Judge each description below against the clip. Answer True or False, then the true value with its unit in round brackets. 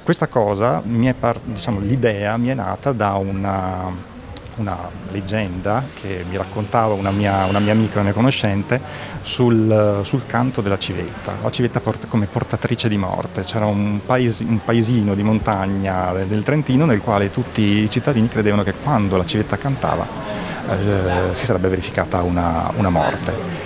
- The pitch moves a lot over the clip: False (3.3 semitones)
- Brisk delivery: False (150 wpm)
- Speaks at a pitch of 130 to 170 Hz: False (105 Hz)